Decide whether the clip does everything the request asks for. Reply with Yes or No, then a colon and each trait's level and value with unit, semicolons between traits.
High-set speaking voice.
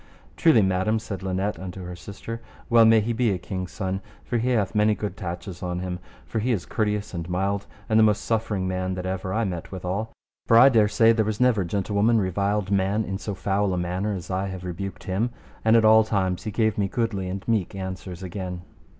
No: low, 100 Hz